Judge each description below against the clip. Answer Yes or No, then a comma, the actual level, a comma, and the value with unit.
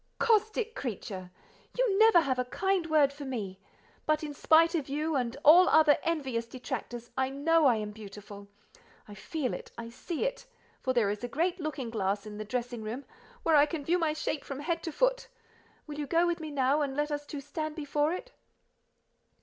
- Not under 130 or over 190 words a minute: No, average, 200 wpm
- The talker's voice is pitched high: Yes, very high, 290 Hz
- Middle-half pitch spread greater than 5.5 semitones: No, average, 5.2 semitones